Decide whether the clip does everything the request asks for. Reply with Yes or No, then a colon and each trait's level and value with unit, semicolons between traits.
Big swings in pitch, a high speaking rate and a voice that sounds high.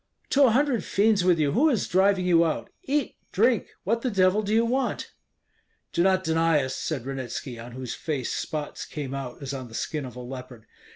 No: wide, 8.2 semitones; fast, 210 wpm; medium, 165 Hz